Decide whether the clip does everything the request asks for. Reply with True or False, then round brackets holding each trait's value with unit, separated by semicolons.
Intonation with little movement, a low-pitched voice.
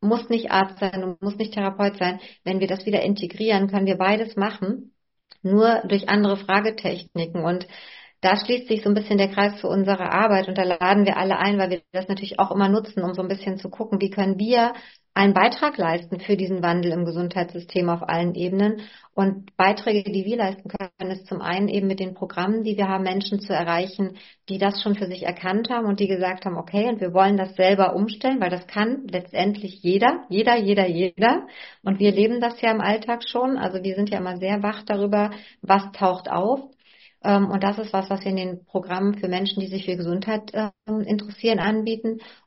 False (2.1 semitones; 195 Hz)